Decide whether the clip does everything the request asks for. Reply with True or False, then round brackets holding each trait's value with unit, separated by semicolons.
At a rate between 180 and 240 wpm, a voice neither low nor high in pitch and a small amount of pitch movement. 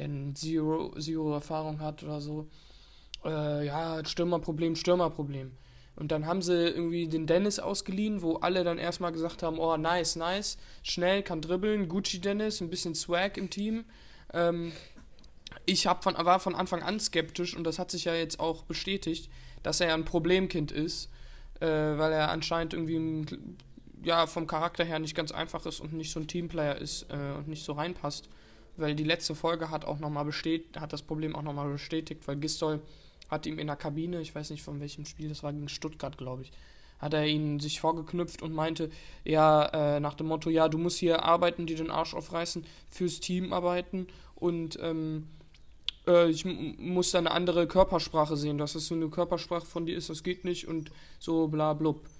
True (190 wpm; 160 Hz; 2.1 semitones)